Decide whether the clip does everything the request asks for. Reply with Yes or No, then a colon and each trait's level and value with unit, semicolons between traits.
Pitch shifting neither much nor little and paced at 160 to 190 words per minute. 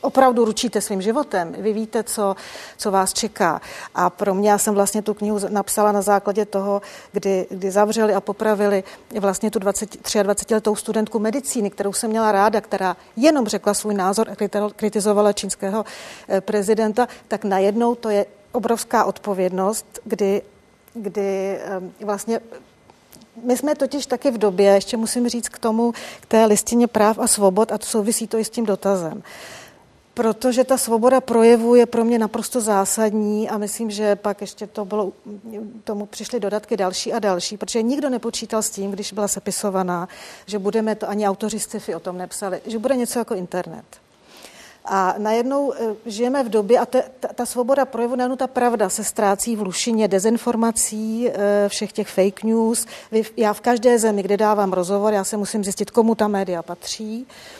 No: narrow, 2.3 semitones; average, 165 wpm